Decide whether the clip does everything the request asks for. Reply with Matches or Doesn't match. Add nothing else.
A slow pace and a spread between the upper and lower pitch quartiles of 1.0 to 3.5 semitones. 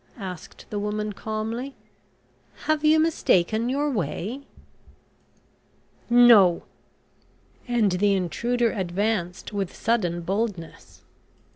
Doesn't match